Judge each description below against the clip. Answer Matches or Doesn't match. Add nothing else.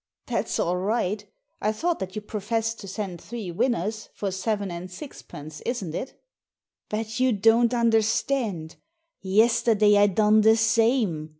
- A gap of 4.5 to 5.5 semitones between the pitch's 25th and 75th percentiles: Doesn't match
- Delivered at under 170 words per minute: Matches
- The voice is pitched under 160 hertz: Doesn't match